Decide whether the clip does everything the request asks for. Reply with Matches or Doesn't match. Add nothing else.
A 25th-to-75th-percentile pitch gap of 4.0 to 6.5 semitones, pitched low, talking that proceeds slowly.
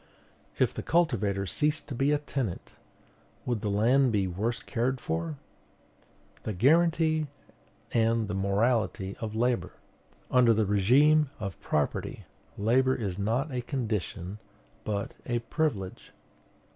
Matches